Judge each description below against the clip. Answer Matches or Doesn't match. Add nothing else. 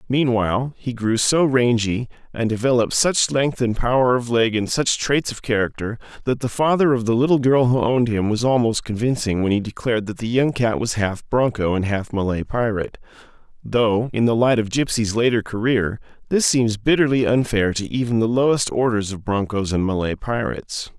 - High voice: Doesn't match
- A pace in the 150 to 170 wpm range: Doesn't match